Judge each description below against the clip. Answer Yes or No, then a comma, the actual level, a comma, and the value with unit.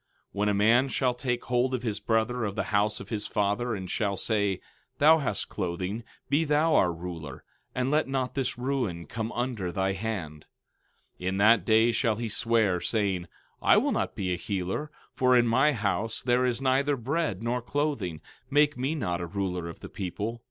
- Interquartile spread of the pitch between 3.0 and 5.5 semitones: Yes, average, 4.7 semitones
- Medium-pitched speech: No, low, 115 Hz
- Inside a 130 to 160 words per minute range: No, average, 195 wpm